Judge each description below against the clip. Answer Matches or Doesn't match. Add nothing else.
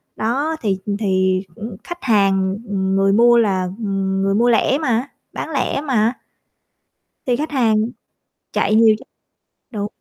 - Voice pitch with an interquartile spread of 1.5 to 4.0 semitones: Matches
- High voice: Matches